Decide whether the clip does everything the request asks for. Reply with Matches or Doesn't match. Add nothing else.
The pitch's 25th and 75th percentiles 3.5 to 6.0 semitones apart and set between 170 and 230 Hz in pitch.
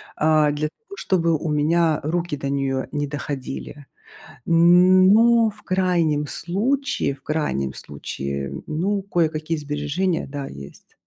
Doesn't match